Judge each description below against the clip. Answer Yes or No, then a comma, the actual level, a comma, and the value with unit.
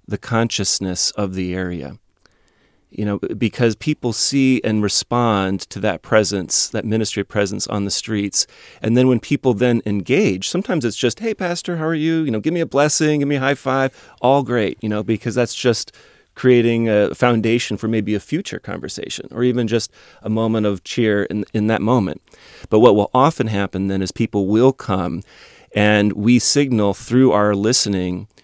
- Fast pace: No, average, 185 wpm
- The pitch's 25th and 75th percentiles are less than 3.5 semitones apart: No, average, 3.8 semitones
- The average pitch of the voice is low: Yes, low, 110 Hz